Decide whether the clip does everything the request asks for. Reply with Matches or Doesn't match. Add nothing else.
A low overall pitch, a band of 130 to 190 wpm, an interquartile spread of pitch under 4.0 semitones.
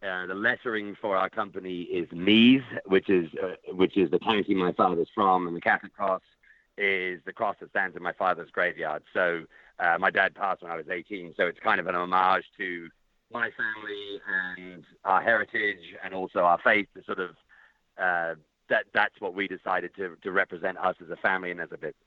Doesn't match